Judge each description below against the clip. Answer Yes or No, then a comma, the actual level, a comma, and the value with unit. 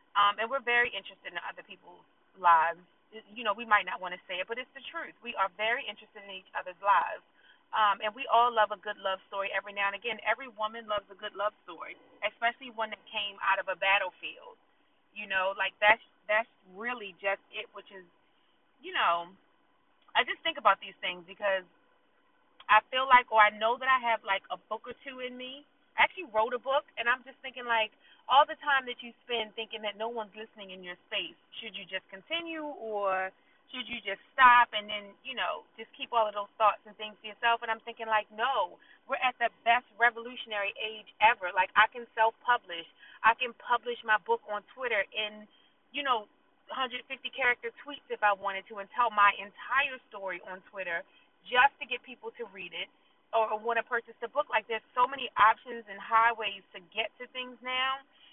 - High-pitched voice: Yes, high, 220 Hz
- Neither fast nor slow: No, fast, 210 wpm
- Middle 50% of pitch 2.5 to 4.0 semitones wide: Yes, average, 3.6 semitones